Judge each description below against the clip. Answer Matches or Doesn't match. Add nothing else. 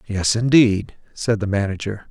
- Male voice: Matches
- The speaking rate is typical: Matches